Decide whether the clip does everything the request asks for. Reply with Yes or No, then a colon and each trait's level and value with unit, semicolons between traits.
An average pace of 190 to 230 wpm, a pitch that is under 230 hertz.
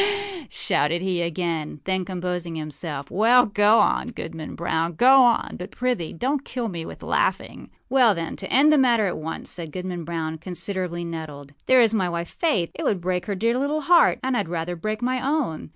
Yes: fast, 205 wpm; medium, 185 Hz